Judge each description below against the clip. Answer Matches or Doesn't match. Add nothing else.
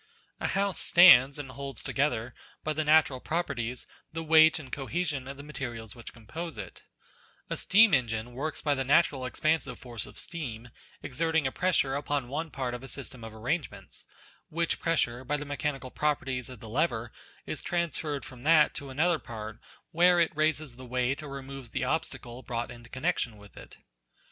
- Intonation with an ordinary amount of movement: Matches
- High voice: Doesn't match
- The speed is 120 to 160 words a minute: Doesn't match